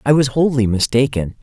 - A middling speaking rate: Yes, average, 170 wpm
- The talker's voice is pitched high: No, low, 125 Hz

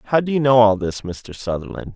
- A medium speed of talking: No, fast, 245 wpm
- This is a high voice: No, low, 110 Hz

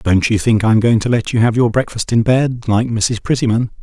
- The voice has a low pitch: Yes, low, 115 Hz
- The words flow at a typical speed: No, fast, 265 wpm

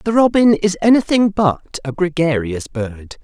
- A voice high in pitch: No, medium, 175 Hz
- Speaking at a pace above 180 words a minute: No, average, 150 wpm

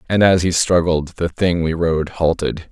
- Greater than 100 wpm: Yes, average, 200 wpm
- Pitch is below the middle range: Yes, very low, 85 Hz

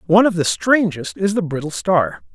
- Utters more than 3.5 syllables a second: Yes, 5.2 syllables/s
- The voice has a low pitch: No, medium, 175 Hz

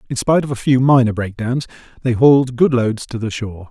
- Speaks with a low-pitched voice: Yes, low, 125 Hz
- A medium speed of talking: No, fast, 225 wpm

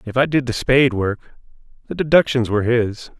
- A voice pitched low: Yes, low, 120 Hz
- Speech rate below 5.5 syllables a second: No, 5.6 syllables/s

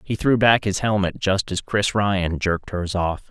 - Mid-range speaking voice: No, low, 100 Hz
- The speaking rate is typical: No, fast, 220 wpm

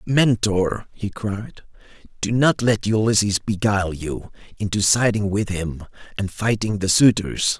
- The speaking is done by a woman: No, male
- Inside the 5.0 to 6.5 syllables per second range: No, 4.2 syllables/s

